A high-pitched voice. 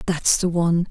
No: medium, 170 Hz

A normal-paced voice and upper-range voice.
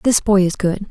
No: fast, 265 wpm; high, 195 Hz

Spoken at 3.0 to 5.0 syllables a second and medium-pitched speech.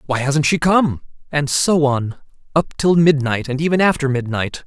Yes: 4.7 syllables/s; medium, 145 Hz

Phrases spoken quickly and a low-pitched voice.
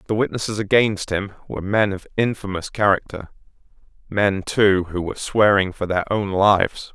No: average, 155 wpm; low, 100 Hz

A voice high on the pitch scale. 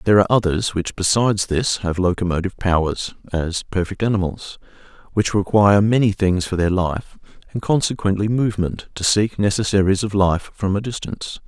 No: low, 100 Hz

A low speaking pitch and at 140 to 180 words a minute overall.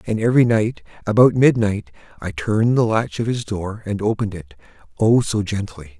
Yes: low, 105 Hz; average, 170 wpm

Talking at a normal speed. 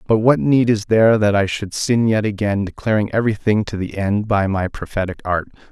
No: fast, 210 wpm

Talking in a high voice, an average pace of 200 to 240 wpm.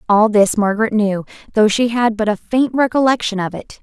Yes: high, 220 Hz; fast, 205 wpm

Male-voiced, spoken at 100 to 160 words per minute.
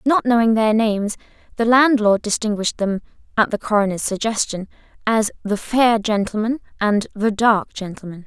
No: female; average, 145 wpm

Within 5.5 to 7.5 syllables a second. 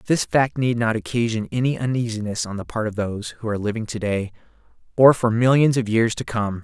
Yes: 5.7 syllables/s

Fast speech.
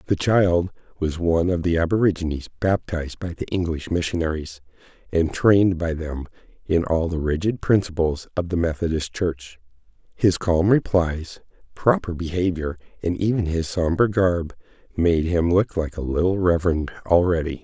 No: average, 145 wpm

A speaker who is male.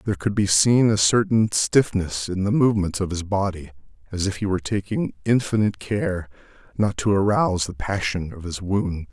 Yes: male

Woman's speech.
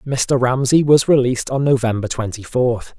No: male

